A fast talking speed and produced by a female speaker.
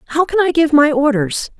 Yes: fast, 225 wpm; female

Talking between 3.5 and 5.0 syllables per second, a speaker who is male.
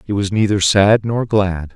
Yes: 4.4 syllables/s; male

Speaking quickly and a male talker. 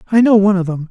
Yes: fast, 330 wpm; male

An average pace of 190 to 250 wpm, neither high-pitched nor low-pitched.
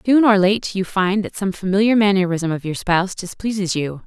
No: fast, 205 wpm; high, 195 Hz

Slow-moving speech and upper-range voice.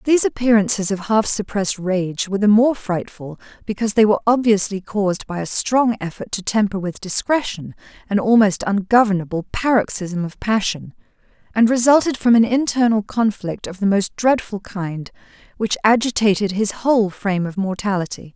No: average, 155 wpm; high, 210 Hz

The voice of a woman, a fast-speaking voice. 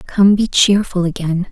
No: female; average, 160 wpm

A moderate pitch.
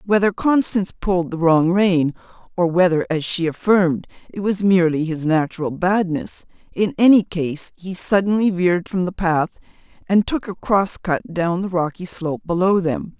Yes: medium, 180 Hz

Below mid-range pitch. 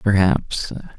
Yes: low, 100 Hz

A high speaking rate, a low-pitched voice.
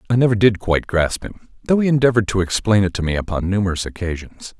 Yes: fast, 220 wpm; low, 100 Hz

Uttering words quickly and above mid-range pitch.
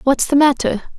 No: average, 185 wpm; very high, 270 Hz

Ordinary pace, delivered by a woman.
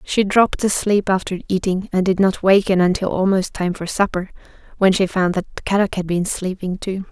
Yes: average, 195 wpm; female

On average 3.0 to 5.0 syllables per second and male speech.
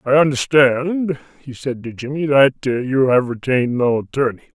Yes: 4.8 syllables/s; male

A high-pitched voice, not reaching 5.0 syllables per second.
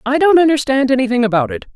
No: very high, 255 Hz; 7.0 syllables/s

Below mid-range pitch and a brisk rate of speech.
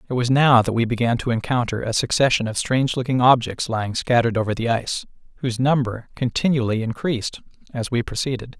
No: low, 120 Hz; average, 180 wpm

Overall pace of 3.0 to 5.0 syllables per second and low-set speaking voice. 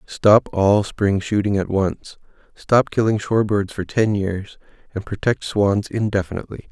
Yes: 4.5 syllables/s; low, 100 Hz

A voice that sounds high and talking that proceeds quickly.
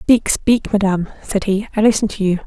Yes: high, 205 Hz; fast, 220 wpm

